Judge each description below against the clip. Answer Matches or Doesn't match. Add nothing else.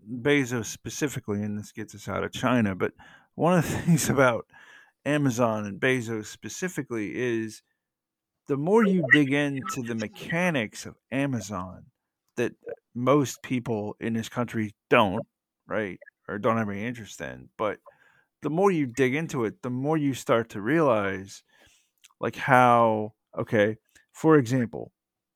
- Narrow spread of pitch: Doesn't match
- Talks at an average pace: Matches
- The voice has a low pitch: Matches